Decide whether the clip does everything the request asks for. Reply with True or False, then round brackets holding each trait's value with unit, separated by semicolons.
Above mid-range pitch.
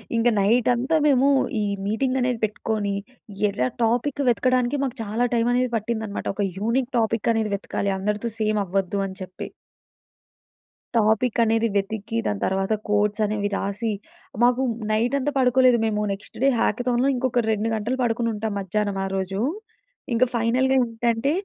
True (225 Hz)